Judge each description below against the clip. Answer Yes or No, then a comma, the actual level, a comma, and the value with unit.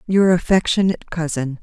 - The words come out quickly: No, slow, 110 wpm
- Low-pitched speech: No, medium, 170 Hz